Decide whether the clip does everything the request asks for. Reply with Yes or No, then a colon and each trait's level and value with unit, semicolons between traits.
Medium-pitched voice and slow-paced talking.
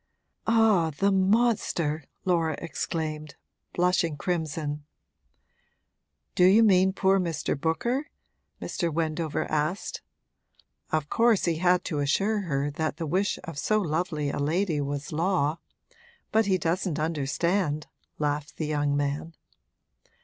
Yes: medium, 165 Hz; slow, 120 wpm